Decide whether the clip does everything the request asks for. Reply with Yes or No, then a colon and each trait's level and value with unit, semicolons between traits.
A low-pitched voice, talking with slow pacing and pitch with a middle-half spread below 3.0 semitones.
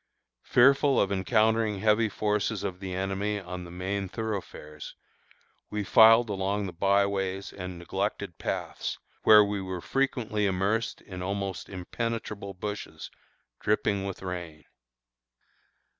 Yes: low, 100 Hz; slow, 125 wpm; narrow, 2.4 semitones